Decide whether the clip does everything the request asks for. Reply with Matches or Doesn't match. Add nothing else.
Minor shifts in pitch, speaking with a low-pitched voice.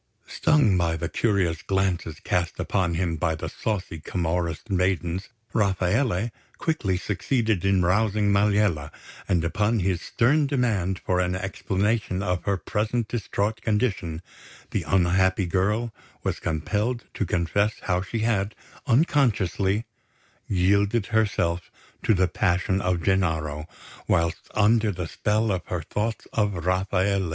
Doesn't match